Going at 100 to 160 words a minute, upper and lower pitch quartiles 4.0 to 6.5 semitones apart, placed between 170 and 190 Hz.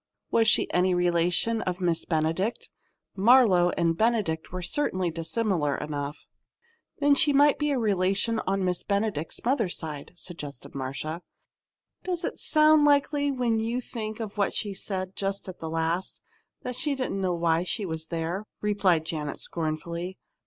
Yes: average, 155 wpm; wide, 5.5 semitones; medium, 185 Hz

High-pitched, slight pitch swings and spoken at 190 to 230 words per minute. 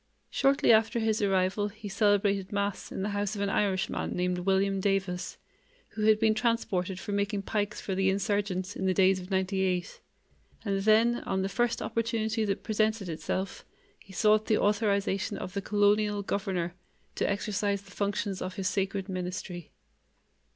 No: high, 200 Hz; narrow, 1.8 semitones; average, 165 wpm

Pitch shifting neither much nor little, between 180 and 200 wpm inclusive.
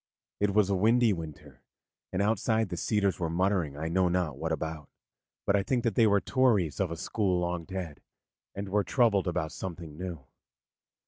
Yes: average, 3.8 semitones; average, 185 wpm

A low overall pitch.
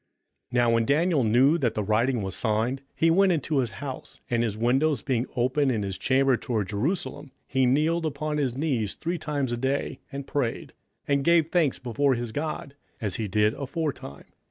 Yes: low, 130 Hz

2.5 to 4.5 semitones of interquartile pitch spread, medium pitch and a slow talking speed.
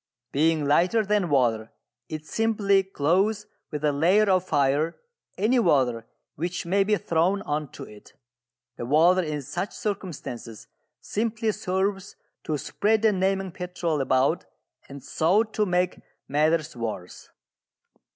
No: wide, 5.4 semitones; medium, 175 Hz; slow, 130 wpm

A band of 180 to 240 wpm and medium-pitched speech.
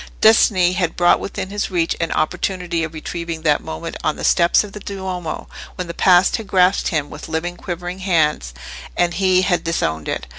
Yes: average, 190 wpm; medium, 175 Hz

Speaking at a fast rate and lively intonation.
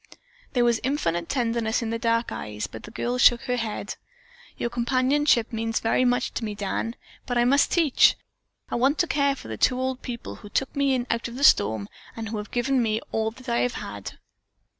No: fast, 215 wpm; narrow, 2.5 semitones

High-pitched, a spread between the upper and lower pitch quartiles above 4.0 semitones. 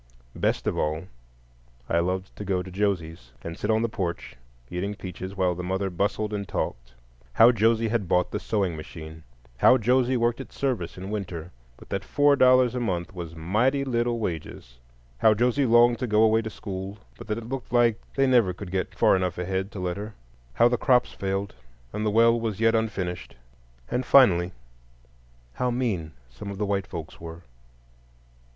No: low, 100 Hz; average, 4.6 semitones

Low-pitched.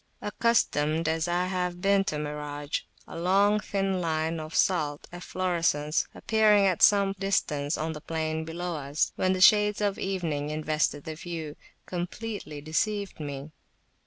No: medium, 170 Hz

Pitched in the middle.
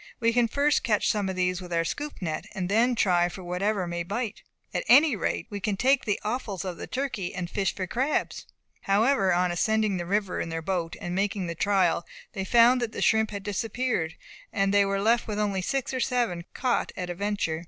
No: high, 200 Hz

